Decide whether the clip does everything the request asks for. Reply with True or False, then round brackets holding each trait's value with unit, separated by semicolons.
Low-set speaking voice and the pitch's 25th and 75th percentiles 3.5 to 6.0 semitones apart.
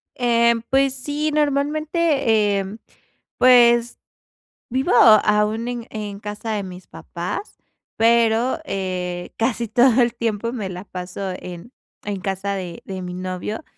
False (220 Hz; 4.2 semitones)